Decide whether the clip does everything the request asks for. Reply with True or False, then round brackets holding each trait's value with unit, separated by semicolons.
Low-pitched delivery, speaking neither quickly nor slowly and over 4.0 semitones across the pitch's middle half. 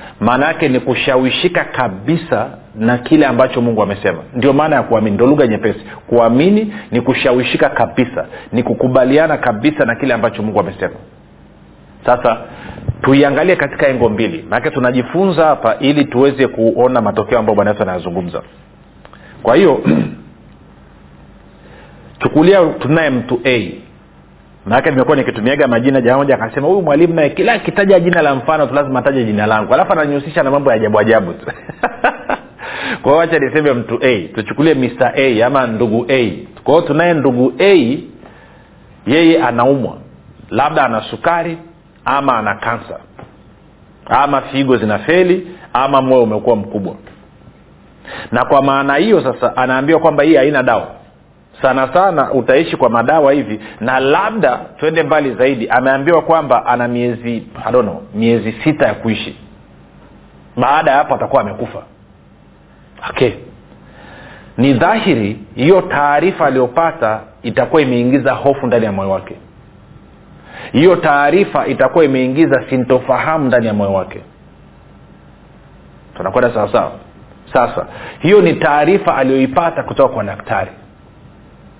True (130 Hz; 130 wpm; 5.4 semitones)